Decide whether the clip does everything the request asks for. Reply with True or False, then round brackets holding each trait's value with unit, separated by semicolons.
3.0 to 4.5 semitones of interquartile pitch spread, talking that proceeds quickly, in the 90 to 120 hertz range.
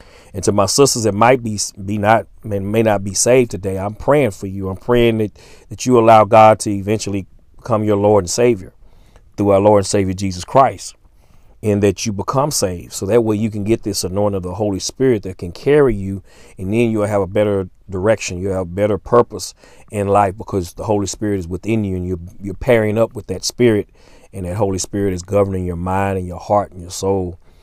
False (2.5 semitones; 225 wpm; 100 Hz)